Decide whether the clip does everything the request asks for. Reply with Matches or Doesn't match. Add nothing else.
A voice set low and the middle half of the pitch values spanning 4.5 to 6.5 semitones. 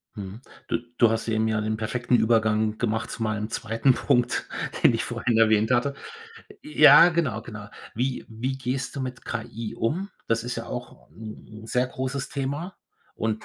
Doesn't match